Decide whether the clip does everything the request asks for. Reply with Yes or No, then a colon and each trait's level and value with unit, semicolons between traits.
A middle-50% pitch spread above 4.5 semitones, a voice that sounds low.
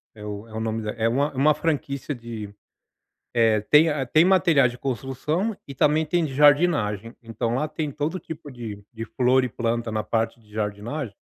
Yes: average, 4.9 semitones; low, 125 Hz